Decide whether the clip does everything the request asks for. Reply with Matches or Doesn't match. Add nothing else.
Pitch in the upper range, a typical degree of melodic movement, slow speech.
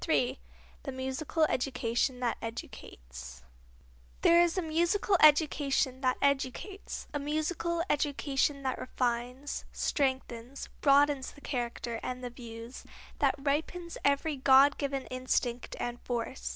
Matches